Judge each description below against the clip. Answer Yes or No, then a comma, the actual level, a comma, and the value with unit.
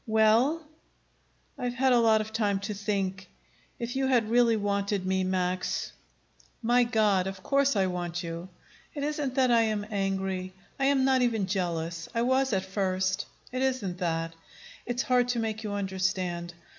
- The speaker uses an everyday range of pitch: Yes, average, 4.6 semitones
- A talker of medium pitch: No, high, 210 Hz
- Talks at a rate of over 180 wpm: No, average, 170 wpm